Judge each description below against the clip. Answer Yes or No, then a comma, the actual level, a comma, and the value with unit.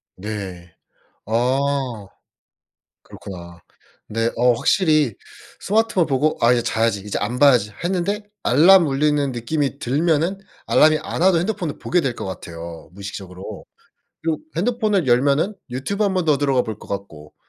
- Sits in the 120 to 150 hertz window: Yes, low, 135 Hz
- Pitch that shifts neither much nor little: No, wide, 7.4 semitones